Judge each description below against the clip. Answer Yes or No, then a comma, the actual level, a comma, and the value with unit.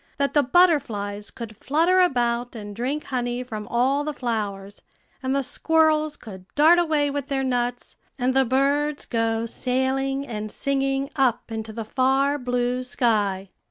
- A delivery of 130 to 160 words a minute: Yes, average, 155 wpm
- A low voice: No, very high, 255 Hz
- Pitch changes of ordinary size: Yes, average, 3.6 semitones